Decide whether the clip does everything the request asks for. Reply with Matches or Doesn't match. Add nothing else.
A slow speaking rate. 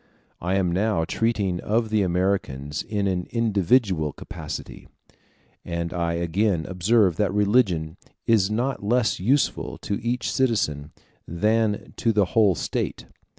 Matches